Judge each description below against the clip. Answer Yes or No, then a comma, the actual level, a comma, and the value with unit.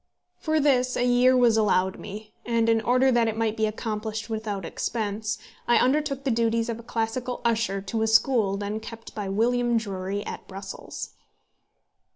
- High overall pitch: Yes, high, 225 Hz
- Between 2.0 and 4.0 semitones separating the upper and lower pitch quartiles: Yes, narrow, 2.5 semitones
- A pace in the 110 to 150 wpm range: No, average, 175 wpm